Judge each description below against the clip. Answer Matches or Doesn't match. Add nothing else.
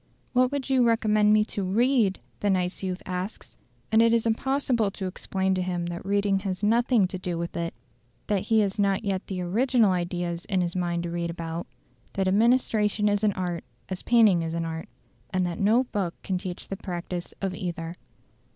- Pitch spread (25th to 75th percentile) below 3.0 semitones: Doesn't match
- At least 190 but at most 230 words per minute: Matches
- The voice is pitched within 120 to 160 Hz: Doesn't match